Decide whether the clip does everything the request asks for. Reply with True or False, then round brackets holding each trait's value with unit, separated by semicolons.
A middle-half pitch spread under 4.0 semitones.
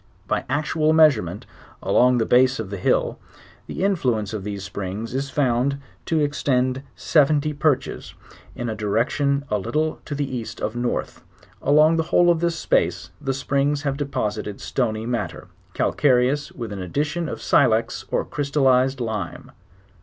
False (4.8 semitones)